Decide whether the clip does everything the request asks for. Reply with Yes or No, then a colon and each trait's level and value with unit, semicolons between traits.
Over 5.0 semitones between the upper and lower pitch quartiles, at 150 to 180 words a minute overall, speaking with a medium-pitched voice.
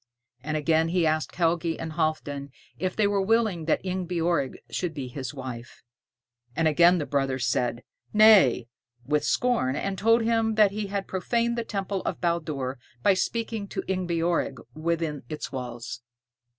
Yes: wide, 5.4 semitones; average, 155 wpm; medium, 170 Hz